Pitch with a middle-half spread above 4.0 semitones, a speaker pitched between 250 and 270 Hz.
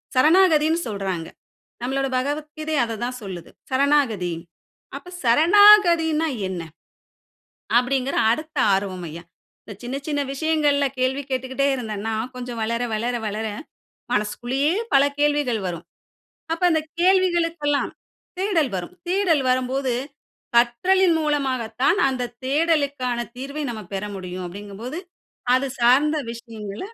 Yes: average, 5.1 semitones; very high, 265 Hz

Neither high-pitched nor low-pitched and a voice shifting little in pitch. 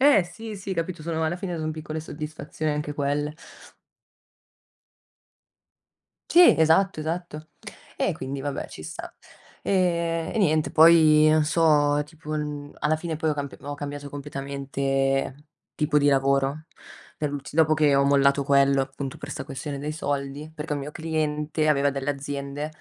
Yes: medium, 150 Hz; narrow, 2.1 semitones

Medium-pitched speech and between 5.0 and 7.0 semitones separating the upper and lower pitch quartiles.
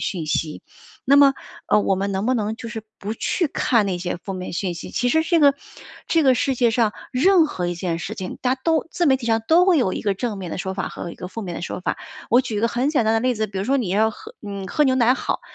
No: high, 225 Hz; wide, 5.6 semitones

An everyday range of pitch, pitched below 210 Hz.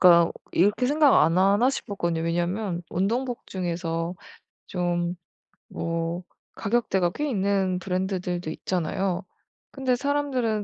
Yes: average, 4.5 semitones; medium, 185 Hz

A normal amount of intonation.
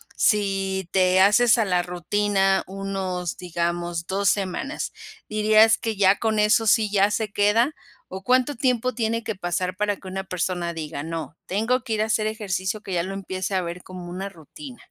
Yes: average, 3.0 semitones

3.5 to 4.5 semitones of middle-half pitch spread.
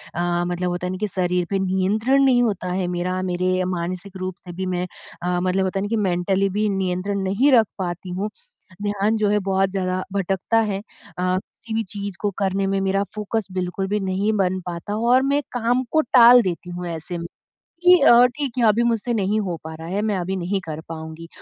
No: average, 2.7 semitones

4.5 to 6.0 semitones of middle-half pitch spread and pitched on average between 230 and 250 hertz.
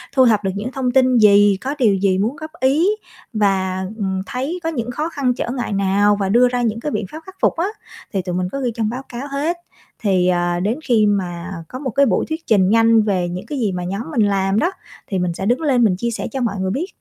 No: average, 5.2 semitones; high, 220 Hz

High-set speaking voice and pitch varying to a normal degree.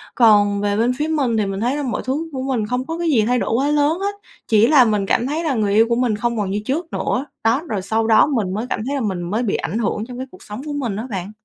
Yes: high, 235 Hz; average, 4.6 semitones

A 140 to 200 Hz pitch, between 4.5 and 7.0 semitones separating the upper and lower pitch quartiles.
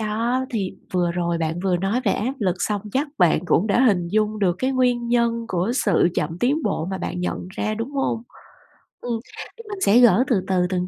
No: high, 215 Hz; average, 5.1 semitones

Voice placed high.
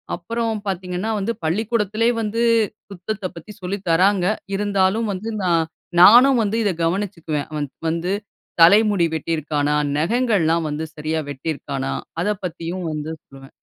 No: medium, 180 Hz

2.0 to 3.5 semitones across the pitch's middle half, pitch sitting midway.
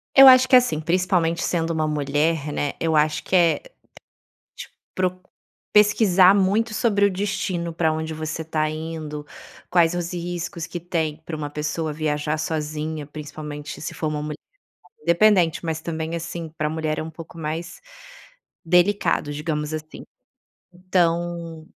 Yes: narrow, 2.4 semitones; medium, 165 Hz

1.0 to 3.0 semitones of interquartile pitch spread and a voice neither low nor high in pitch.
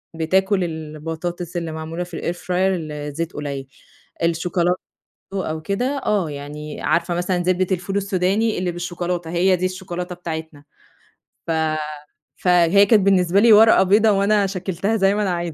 Yes: average, 2.7 semitones; medium, 180 Hz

